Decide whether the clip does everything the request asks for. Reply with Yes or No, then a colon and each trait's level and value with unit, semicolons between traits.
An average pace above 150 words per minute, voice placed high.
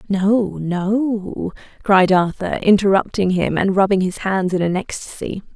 No: average, 140 wpm; high, 195 Hz